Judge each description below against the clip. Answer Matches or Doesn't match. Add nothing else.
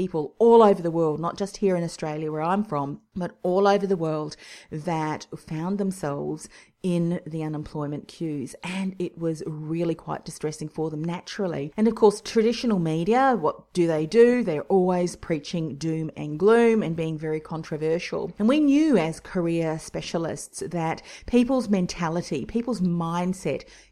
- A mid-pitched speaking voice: Matches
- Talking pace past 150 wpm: Matches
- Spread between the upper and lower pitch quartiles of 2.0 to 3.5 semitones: Doesn't match